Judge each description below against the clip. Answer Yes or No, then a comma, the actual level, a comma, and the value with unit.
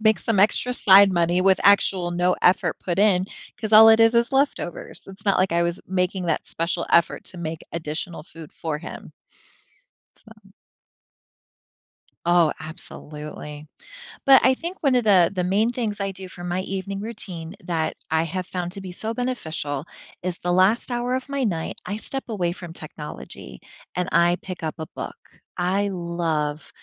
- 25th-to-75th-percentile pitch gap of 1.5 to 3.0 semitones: No, average, 3.6 semitones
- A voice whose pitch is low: No, medium, 185 Hz